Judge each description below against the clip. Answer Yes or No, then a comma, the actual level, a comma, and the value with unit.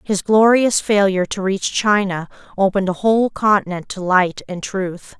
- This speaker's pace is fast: No, average, 160 wpm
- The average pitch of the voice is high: Yes, high, 195 Hz